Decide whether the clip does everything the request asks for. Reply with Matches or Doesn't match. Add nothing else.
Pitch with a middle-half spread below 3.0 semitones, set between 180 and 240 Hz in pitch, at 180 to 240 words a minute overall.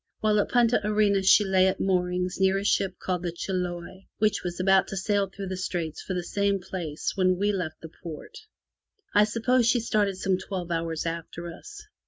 Matches